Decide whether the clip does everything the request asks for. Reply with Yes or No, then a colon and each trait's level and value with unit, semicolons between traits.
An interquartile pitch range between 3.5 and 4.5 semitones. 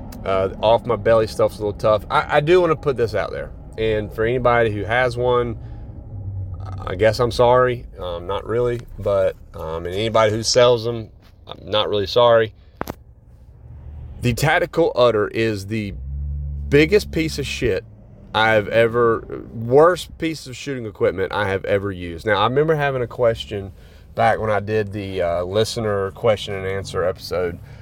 Yes: average, 3.8 semitones